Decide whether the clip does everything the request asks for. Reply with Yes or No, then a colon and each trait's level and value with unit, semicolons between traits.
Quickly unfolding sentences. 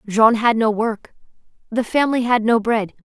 No: average, 175 wpm